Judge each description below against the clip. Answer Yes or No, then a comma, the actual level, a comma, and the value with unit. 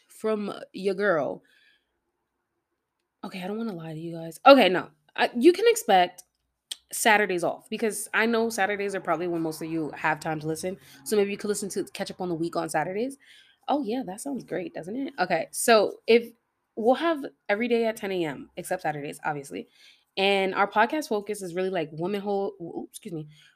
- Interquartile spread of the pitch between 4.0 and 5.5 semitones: Yes, average, 4.9 semitones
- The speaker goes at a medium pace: Yes, average, 195 wpm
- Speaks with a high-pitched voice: Yes, high, 200 Hz